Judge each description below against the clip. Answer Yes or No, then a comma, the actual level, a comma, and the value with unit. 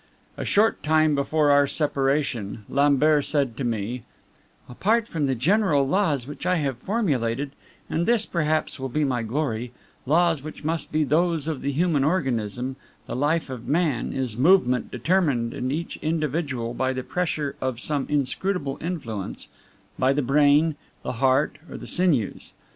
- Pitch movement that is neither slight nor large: Yes, average, 3.9 semitones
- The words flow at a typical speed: Yes, average, 160 wpm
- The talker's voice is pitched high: No, medium, 145 Hz